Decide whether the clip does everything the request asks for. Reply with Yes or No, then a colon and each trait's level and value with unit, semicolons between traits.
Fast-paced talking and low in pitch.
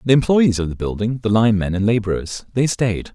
Yes: fast, 210 wpm; low, 110 Hz